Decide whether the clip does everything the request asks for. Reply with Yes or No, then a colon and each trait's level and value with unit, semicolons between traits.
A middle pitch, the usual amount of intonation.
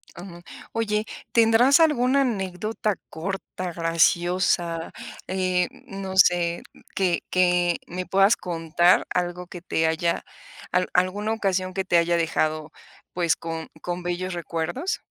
No: medium, 180 Hz; narrow, 2.3 semitones